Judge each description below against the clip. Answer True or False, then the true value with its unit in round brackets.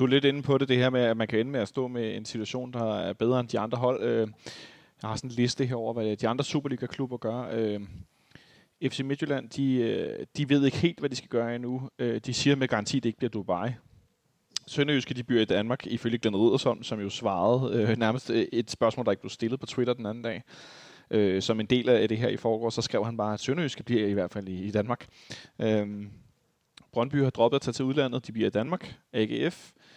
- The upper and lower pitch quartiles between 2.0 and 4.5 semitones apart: True (2.9 semitones)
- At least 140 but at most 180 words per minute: False (225 wpm)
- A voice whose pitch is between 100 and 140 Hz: True (120 Hz)